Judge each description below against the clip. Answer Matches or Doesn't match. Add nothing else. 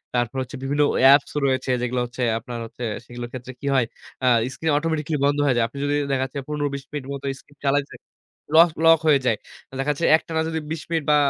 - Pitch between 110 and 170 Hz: Matches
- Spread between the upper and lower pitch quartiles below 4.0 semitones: Matches